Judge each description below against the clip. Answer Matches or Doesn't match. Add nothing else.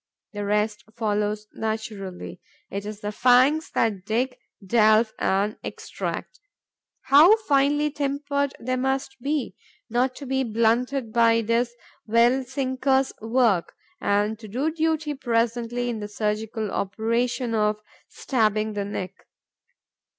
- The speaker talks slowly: Matches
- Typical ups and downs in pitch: Matches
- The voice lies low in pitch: Doesn't match